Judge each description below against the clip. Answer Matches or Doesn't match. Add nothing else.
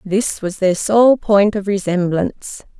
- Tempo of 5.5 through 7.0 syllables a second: Doesn't match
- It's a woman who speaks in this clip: Matches